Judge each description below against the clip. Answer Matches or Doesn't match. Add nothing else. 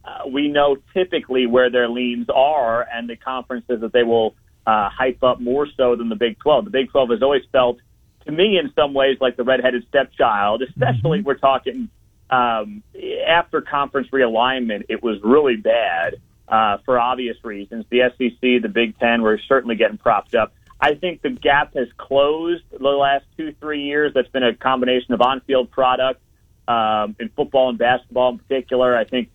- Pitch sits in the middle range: Doesn't match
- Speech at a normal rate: Matches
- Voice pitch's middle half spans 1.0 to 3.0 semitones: Matches